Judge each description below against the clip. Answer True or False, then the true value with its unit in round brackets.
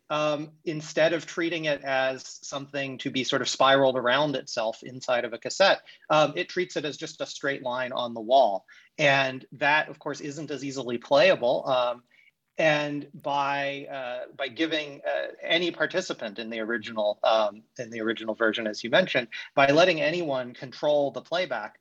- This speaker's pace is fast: False (175 wpm)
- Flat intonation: False (3.3 semitones)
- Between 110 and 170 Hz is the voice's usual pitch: True (140 Hz)